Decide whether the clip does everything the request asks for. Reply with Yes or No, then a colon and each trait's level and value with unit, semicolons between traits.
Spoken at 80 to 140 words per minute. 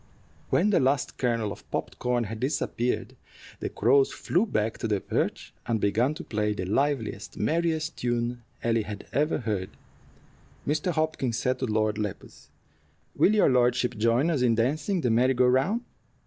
No: average, 165 wpm